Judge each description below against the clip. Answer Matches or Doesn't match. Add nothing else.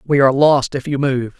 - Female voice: Doesn't match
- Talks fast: Matches